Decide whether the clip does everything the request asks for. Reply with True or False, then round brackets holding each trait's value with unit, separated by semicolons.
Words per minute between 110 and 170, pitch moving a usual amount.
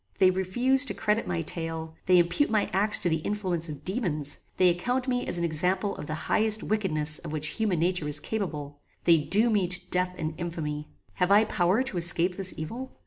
False (200 wpm; 4.6 semitones)